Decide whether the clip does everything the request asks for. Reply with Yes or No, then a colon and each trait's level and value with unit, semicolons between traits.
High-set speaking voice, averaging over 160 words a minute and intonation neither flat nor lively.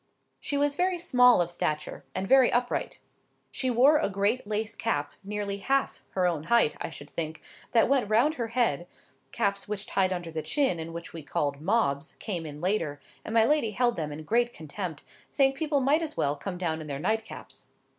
No: high, 200 Hz; average, 200 wpm; wide, 7.3 semitones